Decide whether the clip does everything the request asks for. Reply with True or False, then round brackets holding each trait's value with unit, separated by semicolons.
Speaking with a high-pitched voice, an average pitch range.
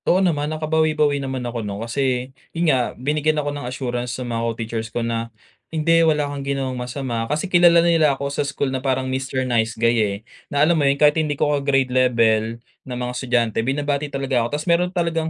False (135 Hz; 3.5 semitones)